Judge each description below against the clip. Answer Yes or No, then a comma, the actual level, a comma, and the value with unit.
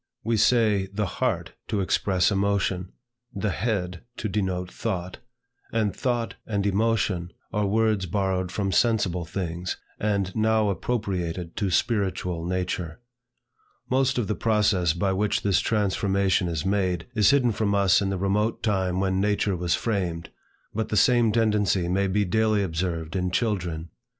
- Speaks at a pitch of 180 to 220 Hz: No, low, 100 Hz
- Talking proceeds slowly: No, average, 150 wpm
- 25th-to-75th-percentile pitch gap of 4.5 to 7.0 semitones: No, average, 2.8 semitones